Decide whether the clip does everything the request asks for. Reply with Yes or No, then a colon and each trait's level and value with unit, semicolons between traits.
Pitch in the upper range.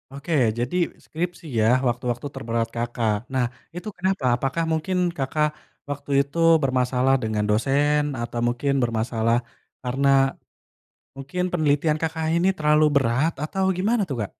No: low, 135 Hz